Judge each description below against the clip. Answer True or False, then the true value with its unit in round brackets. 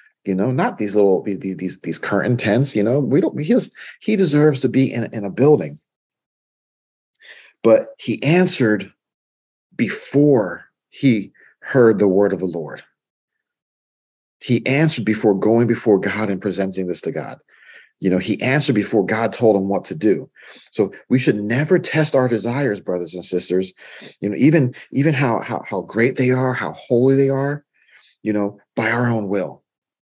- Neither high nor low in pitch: False (115 Hz)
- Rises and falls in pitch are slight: False (5.3 semitones)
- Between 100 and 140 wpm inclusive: False (170 wpm)